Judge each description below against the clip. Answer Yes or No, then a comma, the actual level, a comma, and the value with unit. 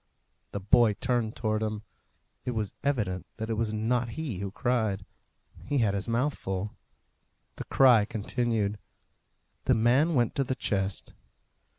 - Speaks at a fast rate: No, average, 150 wpm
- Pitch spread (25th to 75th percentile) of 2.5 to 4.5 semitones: Yes, average, 3.1 semitones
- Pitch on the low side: Yes, low, 110 Hz